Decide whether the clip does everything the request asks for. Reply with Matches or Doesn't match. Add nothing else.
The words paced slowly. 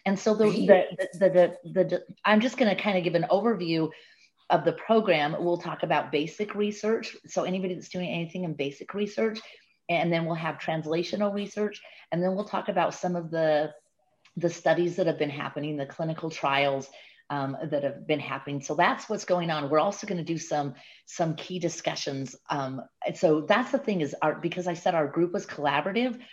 Doesn't match